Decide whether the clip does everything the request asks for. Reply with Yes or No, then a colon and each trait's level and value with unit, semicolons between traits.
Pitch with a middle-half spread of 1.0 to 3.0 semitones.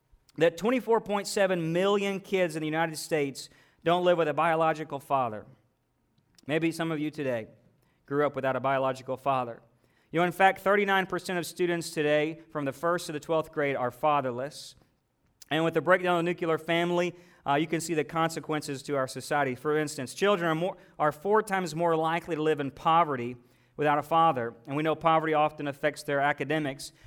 No: average, 3.5 semitones